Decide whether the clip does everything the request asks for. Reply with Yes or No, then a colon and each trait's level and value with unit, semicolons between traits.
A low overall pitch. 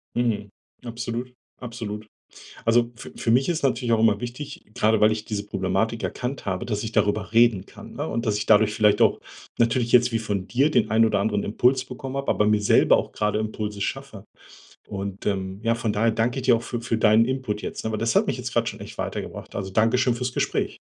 Yes: low, 115 Hz